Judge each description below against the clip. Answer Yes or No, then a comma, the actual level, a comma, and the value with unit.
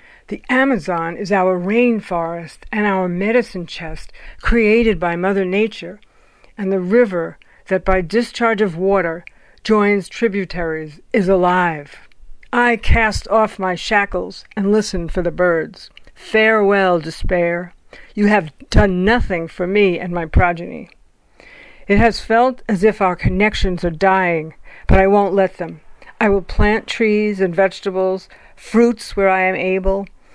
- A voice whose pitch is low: No, high, 195 Hz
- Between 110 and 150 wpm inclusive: Yes, average, 140 wpm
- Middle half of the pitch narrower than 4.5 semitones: Yes, average, 3.3 semitones